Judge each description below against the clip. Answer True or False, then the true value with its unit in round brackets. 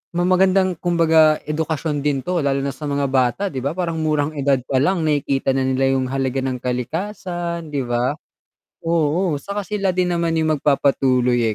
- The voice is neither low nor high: True (150 Hz)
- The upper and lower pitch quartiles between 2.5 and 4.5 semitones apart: True (4.2 semitones)